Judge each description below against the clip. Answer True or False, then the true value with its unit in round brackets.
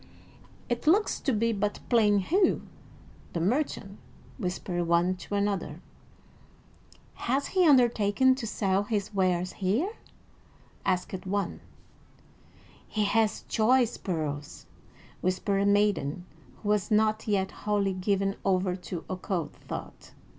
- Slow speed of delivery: True (120 wpm)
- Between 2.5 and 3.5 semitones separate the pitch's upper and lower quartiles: True (3.2 semitones)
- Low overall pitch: False (200 Hz)